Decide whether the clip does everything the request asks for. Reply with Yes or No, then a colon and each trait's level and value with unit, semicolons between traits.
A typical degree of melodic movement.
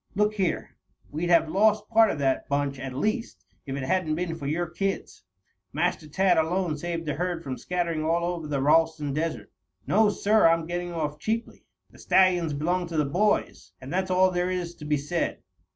Yes: average, 3.4 semitones